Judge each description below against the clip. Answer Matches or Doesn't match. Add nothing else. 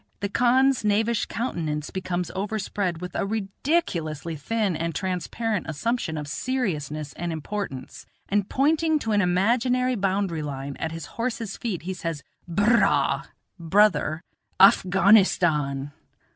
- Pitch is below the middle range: Doesn't match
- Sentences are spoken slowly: Matches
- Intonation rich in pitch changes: Matches